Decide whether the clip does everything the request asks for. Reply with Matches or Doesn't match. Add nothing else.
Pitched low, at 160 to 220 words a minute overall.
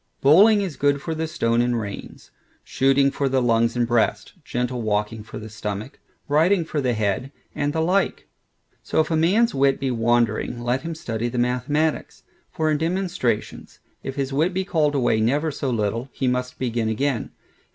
Matches